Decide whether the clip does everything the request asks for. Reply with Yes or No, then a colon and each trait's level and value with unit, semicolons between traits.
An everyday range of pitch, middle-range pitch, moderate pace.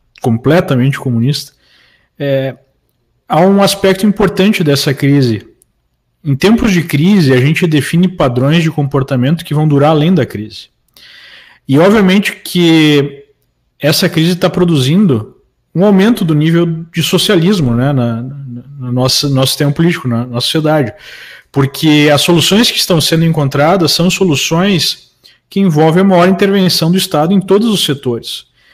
Yes: average, 4.9 semitones; medium, 155 Hz; average, 145 wpm